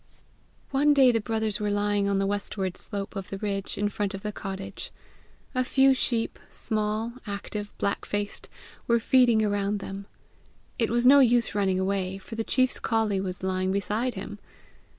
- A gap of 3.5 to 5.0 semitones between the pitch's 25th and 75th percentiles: No, narrow, 2.6 semitones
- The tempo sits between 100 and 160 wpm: No, average, 170 wpm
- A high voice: Yes, high, 205 Hz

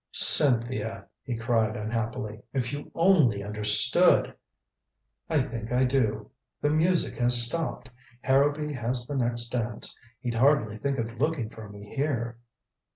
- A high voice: No, low, 120 Hz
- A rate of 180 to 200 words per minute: No, average, 140 wpm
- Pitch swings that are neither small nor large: Yes, average, 3.8 semitones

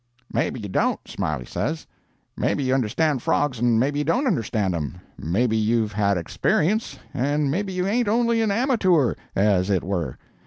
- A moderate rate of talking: Yes, average, 165 wpm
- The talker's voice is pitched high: No, low, 130 Hz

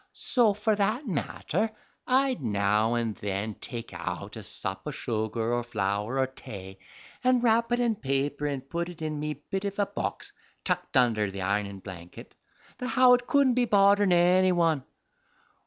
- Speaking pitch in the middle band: Yes, medium, 150 Hz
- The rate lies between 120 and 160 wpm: No, average, 170 wpm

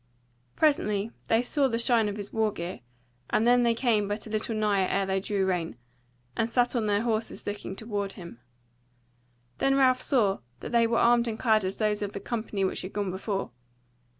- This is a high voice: Yes, high, 215 Hz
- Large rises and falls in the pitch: No, average, 2.9 semitones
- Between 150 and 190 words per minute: No, average, 200 wpm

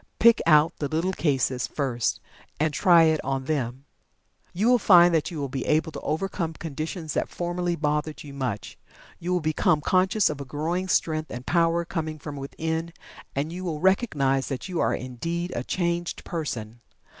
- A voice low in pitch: No, medium, 155 Hz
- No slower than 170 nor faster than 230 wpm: Yes, average, 180 wpm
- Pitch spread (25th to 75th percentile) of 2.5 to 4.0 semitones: Yes, average, 3.6 semitones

